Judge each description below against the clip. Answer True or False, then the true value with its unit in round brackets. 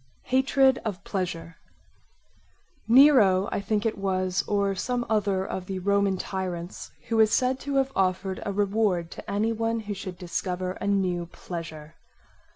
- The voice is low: False (195 Hz)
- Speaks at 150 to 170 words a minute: True (155 wpm)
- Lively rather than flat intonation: False (3.2 semitones)